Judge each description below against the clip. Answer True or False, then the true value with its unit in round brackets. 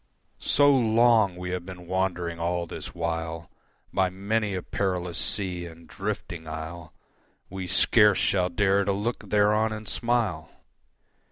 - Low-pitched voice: True (95 Hz)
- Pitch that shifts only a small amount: False (3.4 semitones)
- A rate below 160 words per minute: True (140 wpm)